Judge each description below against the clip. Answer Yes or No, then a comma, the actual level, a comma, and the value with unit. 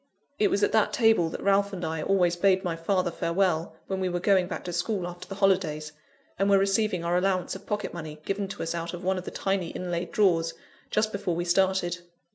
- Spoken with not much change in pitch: Yes, narrow, 2.3 semitones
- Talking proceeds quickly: Yes, fast, 230 wpm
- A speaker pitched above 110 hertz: Yes, medium, 185 Hz